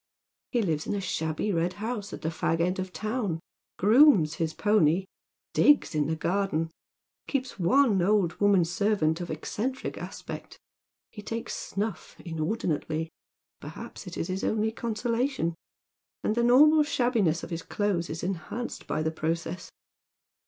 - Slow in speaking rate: No, average, 160 wpm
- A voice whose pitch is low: No, high, 190 Hz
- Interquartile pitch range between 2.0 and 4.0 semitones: No, average, 5.3 semitones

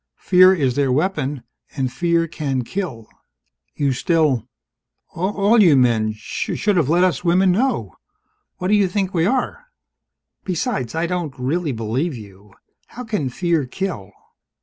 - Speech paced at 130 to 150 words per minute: Yes, average, 145 wpm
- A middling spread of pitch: No, wide, 6.5 semitones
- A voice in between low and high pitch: Yes, medium, 165 Hz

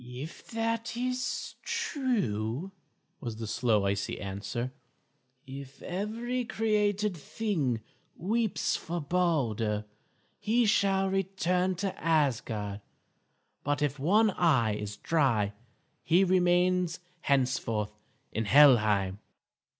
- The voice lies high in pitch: No, medium, 160 Hz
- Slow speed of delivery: Yes, slow, 95 wpm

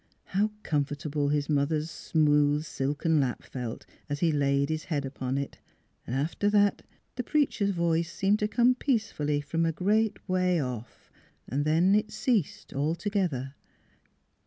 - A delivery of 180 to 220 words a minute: No, slow, 135 wpm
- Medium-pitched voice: Yes, medium, 155 Hz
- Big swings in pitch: Yes, wide, 5.7 semitones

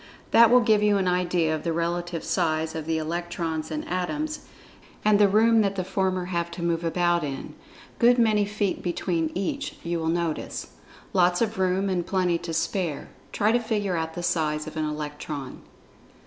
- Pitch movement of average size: Yes, average, 3.6 semitones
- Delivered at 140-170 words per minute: No, average, 180 wpm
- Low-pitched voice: No, medium, 175 Hz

